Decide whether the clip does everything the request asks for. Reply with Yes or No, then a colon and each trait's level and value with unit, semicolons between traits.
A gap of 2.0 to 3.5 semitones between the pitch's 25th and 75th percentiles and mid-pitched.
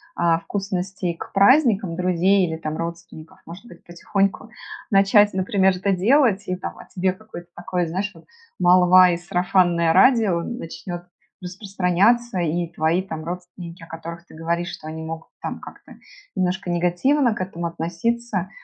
Yes: narrow, 2.5 semitones; medium, 180 Hz